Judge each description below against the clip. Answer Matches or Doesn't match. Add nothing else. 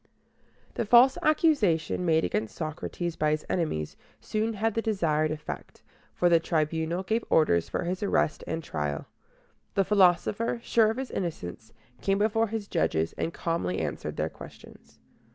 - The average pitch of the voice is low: Doesn't match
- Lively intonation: Matches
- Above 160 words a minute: Doesn't match